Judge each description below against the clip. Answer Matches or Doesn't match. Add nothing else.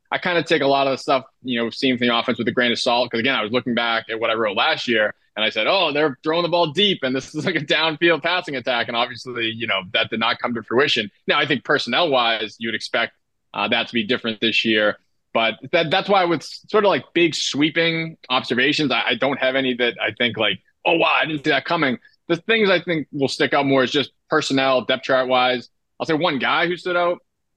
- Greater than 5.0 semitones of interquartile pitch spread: Matches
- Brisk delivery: Matches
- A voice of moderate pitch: Doesn't match